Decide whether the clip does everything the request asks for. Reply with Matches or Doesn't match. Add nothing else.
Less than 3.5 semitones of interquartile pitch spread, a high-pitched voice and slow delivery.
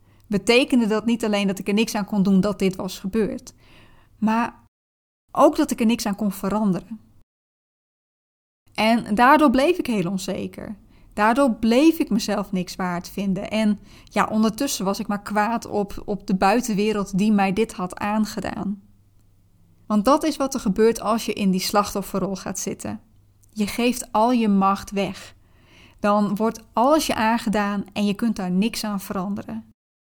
Doesn't match